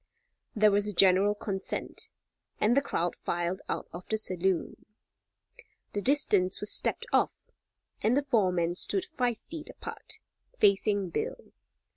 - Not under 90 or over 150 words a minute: Yes, average, 140 wpm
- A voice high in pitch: Yes, high, 205 Hz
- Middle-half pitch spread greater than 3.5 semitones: Yes, average, 4.6 semitones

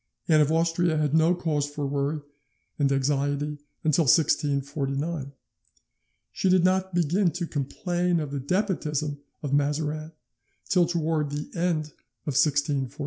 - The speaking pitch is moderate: Yes, medium, 150 Hz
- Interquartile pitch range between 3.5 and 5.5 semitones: No, average, 2.9 semitones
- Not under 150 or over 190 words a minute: No, average, 140 wpm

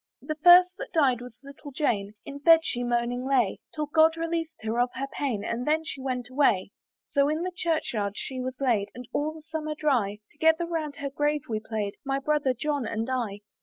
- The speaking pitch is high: Yes, very high, 275 Hz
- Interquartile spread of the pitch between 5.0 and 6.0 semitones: No, average, 4.2 semitones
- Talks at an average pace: No, fast, 210 wpm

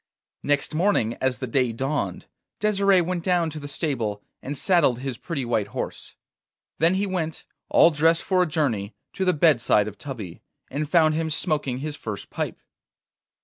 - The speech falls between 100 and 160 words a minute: No, average, 170 wpm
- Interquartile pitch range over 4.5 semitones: Yes, average, 5.2 semitones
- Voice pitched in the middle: Yes, medium, 150 Hz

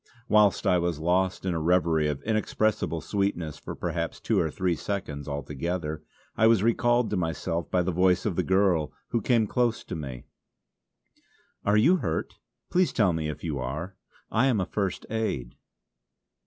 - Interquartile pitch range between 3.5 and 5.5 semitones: Yes, average, 5.2 semitones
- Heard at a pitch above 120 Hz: No, very low, 90 Hz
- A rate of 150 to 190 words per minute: Yes, average, 170 wpm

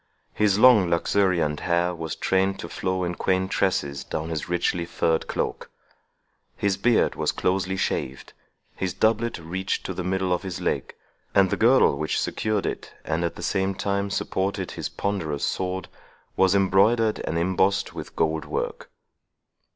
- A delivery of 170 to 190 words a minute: No, average, 160 wpm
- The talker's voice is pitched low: Yes, very low, 95 Hz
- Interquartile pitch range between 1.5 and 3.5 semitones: Yes, narrow, 2.5 semitones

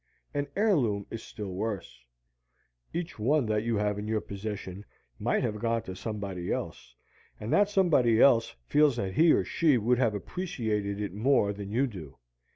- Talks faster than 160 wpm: Yes, average, 170 wpm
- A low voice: Yes, low, 110 Hz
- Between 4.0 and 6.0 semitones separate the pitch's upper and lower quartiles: Yes, average, 4.8 semitones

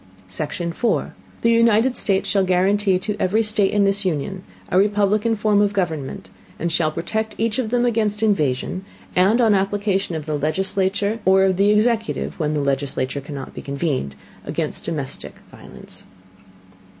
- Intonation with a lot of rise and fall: No, average, 4.6 semitones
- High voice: Yes, high, 195 Hz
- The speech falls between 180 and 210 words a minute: No, average, 160 wpm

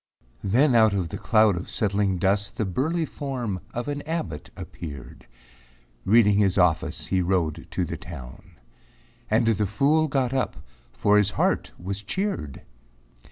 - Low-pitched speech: Yes, low, 105 Hz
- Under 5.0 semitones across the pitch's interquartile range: No, average, 5.3 semitones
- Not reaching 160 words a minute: Yes, average, 150 wpm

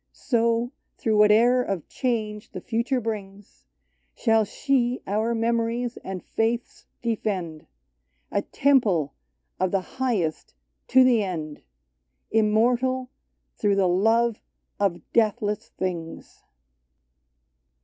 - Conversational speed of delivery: No, slow, 105 wpm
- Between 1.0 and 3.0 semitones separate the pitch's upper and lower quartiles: No, average, 3.6 semitones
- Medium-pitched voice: No, high, 220 Hz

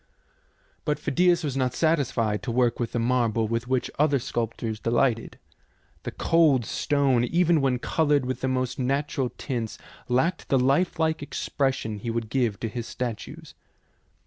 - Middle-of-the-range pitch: No, low, 130 Hz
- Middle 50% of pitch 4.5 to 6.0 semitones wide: No, average, 3.6 semitones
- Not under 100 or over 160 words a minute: Yes, average, 150 wpm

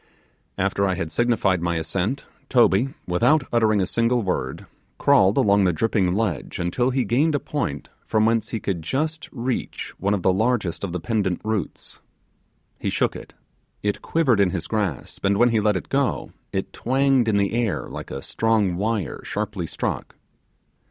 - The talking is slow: No, average, 180 wpm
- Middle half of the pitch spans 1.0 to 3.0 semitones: No, average, 4.4 semitones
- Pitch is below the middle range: Yes, low, 105 Hz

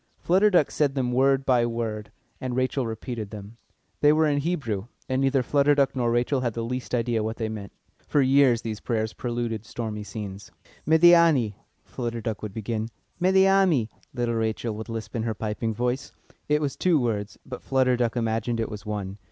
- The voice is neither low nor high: No, low, 120 Hz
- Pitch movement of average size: Yes, average, 3.6 semitones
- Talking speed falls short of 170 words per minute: No, average, 185 wpm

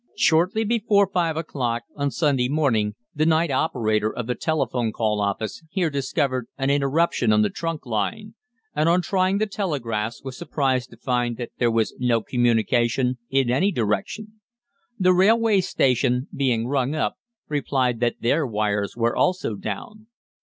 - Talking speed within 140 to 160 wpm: Yes, average, 155 wpm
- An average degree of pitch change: No, wide, 6.0 semitones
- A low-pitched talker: Yes, low, 130 Hz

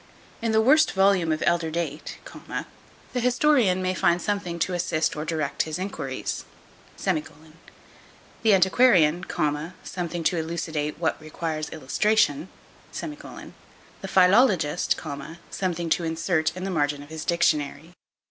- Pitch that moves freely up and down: No, average, 3.4 semitones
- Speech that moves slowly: Yes, slow, 120 wpm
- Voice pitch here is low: No, medium, 170 Hz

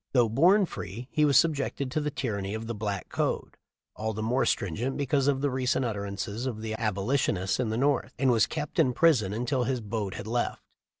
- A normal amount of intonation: Yes, average, 4.2 semitones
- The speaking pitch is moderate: No, low, 120 Hz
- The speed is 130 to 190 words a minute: No, fast, 205 wpm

